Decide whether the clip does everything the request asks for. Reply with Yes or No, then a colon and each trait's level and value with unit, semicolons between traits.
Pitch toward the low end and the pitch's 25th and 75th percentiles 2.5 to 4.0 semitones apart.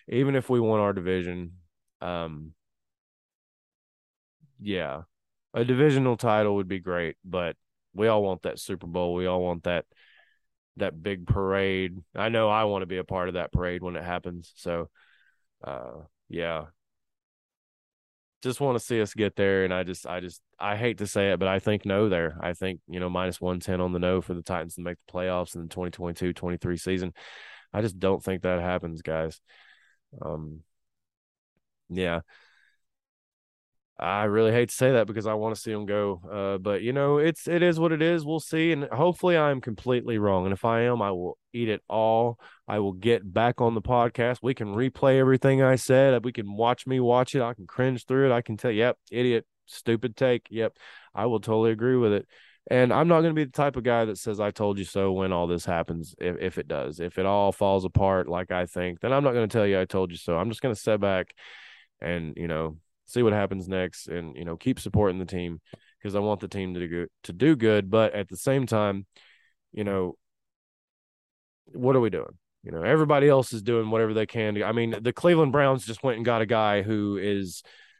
No: low, 100 Hz; average, 4.7 semitones